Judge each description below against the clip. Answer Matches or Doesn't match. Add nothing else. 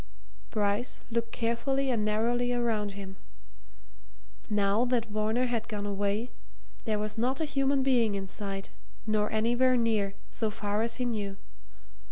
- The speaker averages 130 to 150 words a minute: Matches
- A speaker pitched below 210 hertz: Doesn't match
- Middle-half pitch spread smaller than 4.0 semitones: Matches